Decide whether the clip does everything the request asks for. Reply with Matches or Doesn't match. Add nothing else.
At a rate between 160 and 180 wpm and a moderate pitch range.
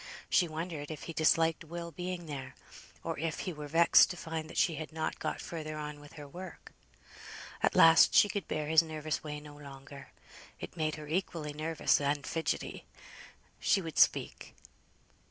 Doesn't match